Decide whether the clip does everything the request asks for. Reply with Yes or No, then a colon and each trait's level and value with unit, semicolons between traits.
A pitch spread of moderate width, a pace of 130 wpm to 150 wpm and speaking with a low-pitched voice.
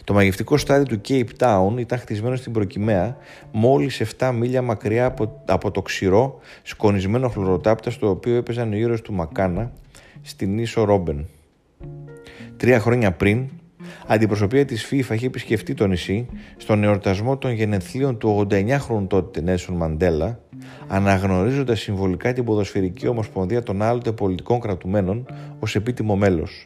Yes: average, 4.3 semitones; average, 135 wpm; low, 110 Hz